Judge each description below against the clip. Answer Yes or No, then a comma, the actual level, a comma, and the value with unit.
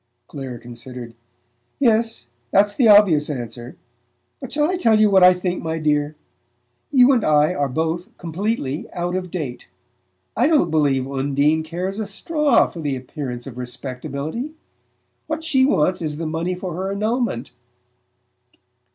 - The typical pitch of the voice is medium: Yes, medium, 165 Hz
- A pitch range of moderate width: No, wide, 7.2 semitones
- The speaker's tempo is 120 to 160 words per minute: Yes, average, 150 wpm